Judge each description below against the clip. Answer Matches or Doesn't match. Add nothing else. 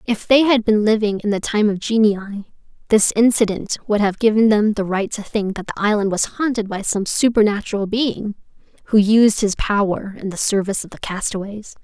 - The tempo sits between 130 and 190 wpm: Doesn't match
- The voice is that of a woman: Matches